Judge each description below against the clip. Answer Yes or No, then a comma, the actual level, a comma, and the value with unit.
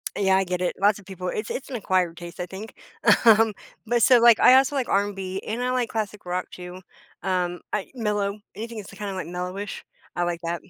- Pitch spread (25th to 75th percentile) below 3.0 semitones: No, average, 3.3 semitones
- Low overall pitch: No, high, 200 Hz